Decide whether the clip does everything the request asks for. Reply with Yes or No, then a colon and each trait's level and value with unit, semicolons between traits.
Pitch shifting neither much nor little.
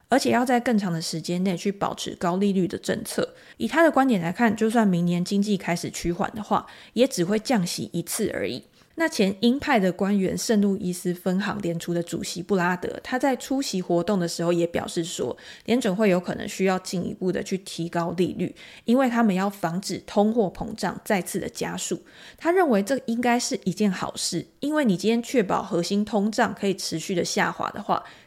Yes: average, 4.5 semitones